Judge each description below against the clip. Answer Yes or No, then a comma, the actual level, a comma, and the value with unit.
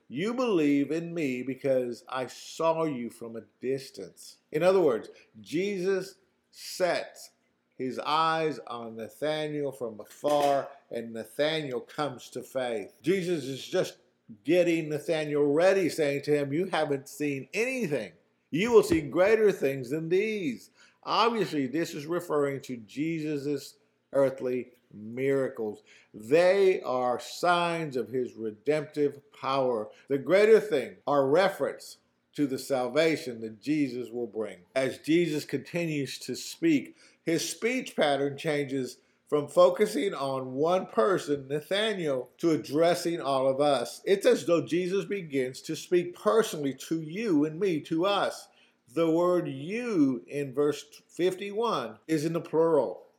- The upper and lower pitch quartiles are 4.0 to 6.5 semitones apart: Yes, average, 4.9 semitones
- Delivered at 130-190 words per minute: Yes, slow, 135 wpm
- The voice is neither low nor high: Yes, medium, 150 Hz